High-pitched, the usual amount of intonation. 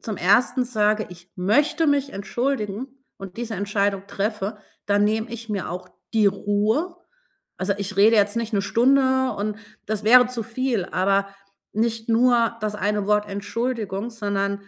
Yes: high, 215 Hz; average, 3.0 semitones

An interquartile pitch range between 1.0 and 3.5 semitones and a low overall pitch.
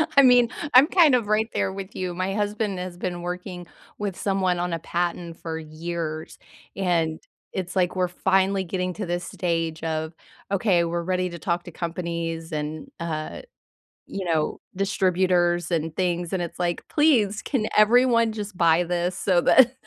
No: narrow, 2.6 semitones; medium, 180 Hz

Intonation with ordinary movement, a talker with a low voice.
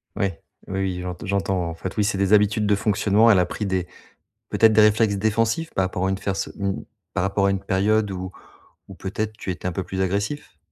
No: narrow, 2.0 semitones; low, 100 Hz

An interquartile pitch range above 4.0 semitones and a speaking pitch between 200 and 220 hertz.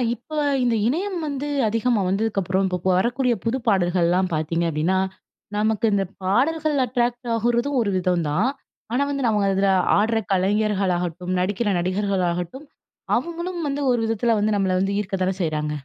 Yes: average, 4.7 semitones; high, 205 Hz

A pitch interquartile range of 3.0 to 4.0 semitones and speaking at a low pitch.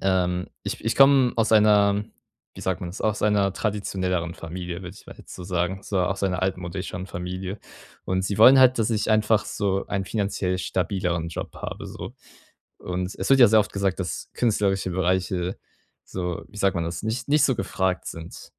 No: narrow, 2.6 semitones; very low, 95 Hz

